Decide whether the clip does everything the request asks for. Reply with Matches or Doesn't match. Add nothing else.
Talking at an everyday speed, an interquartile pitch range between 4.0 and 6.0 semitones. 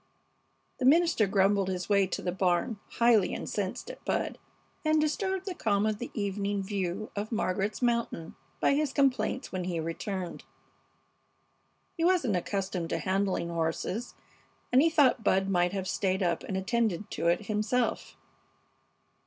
Matches